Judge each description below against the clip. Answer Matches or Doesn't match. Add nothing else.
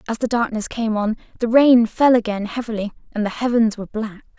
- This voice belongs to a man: Doesn't match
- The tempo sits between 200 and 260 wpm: Matches